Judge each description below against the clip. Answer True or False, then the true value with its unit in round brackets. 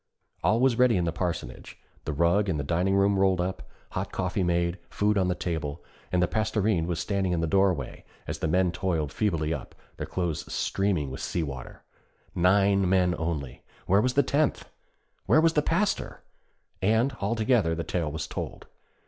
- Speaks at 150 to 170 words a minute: False (185 wpm)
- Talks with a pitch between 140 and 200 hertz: False (90 Hz)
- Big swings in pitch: False (3.7 semitones)